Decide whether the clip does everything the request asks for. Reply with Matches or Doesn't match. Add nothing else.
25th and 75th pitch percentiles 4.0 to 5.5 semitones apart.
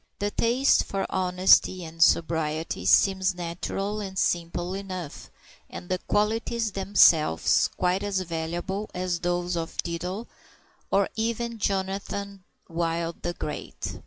Doesn't match